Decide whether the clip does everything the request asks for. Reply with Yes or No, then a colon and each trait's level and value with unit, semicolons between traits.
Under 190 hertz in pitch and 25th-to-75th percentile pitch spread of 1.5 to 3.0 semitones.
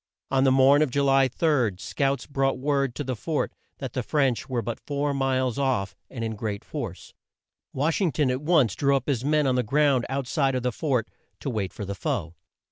Yes: low, 135 Hz; average, 2.7 semitones